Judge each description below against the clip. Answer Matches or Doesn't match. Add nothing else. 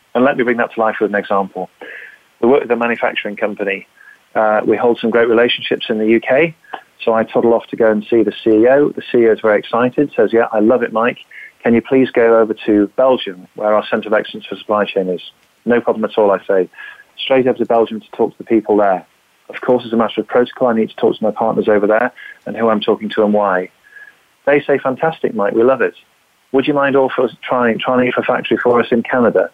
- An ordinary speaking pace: Doesn't match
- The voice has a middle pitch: Doesn't match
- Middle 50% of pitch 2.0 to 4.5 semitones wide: Matches